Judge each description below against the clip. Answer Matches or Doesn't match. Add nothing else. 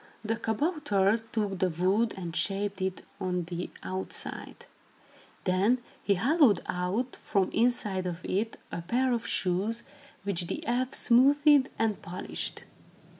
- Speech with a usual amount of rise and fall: Matches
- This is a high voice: Matches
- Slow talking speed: Matches